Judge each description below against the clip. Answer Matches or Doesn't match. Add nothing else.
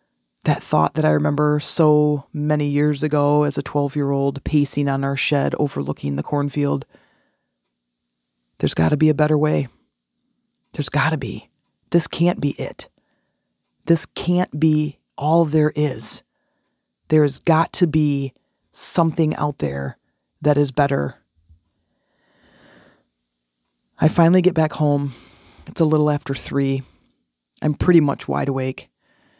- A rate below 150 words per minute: Matches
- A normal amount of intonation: Doesn't match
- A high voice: Doesn't match